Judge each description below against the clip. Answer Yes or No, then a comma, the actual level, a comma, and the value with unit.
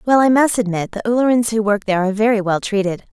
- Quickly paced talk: Yes, fast, 245 wpm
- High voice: Yes, high, 215 Hz